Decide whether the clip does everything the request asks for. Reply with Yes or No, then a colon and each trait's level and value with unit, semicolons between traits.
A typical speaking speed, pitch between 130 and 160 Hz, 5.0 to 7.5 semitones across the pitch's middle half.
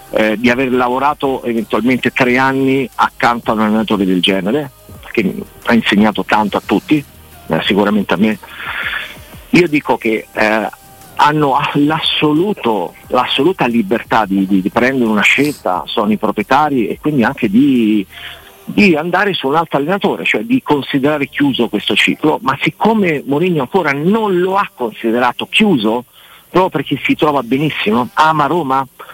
Yes: average, 145 wpm; low, 135 Hz; wide, 5.6 semitones